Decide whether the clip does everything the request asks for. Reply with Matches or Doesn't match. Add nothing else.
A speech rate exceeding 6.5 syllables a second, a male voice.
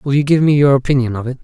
Matches